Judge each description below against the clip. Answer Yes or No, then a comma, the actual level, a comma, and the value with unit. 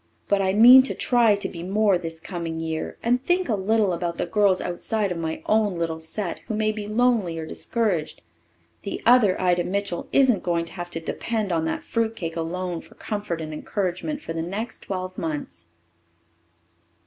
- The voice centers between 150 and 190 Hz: Yes, medium, 185 Hz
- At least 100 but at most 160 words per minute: No, average, 190 wpm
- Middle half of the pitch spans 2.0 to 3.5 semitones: No, average, 4.4 semitones